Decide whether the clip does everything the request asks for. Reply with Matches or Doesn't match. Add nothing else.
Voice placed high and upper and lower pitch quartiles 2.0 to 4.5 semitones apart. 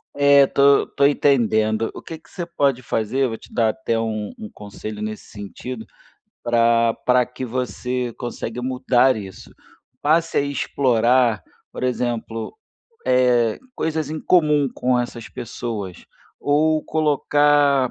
Doesn't match